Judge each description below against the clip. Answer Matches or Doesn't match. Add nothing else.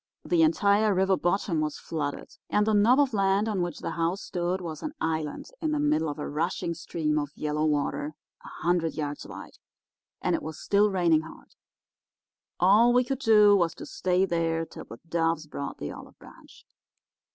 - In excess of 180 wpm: Matches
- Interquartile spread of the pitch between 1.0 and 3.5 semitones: Doesn't match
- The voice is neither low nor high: Matches